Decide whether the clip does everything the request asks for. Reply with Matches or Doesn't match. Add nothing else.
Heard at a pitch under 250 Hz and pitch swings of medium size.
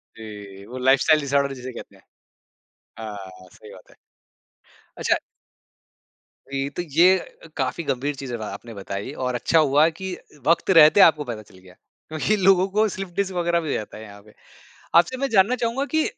Doesn't match